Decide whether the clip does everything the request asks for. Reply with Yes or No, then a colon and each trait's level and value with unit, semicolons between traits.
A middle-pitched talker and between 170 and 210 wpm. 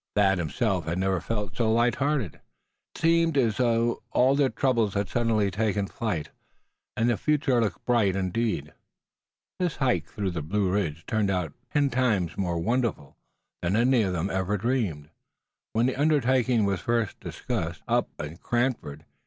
No: low, 110 Hz; average, 175 wpm